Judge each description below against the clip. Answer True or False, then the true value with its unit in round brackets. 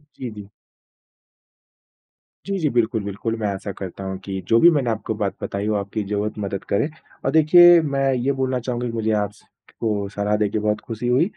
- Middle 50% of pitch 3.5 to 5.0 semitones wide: True (4.3 semitones)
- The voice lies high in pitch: False (110 Hz)